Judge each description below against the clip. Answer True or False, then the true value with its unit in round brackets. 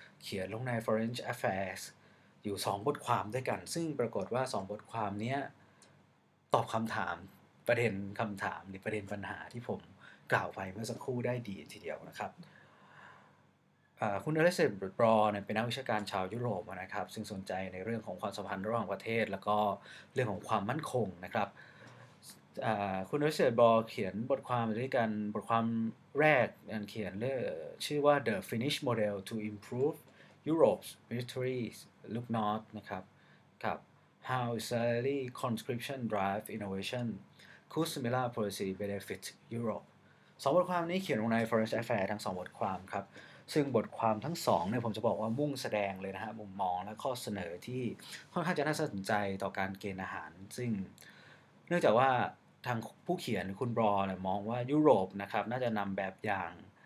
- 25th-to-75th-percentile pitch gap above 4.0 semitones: False (3.5 semitones)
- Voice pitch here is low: True (110 Hz)